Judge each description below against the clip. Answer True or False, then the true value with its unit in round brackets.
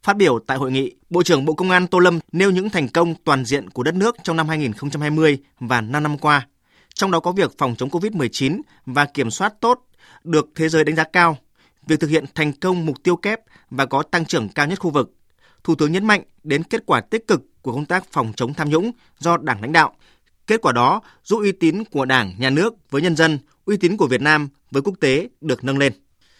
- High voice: False (155 Hz)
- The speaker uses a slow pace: False (240 wpm)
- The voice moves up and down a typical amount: True (4.4 semitones)